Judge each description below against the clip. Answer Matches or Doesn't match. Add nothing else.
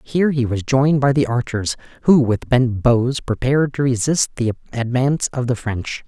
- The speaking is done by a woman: Doesn't match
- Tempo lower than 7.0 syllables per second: Matches